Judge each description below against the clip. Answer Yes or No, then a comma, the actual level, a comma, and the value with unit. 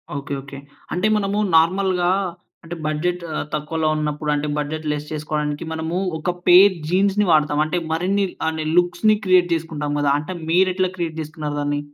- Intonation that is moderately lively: Yes, average, 3.2 semitones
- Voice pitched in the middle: Yes, medium, 160 Hz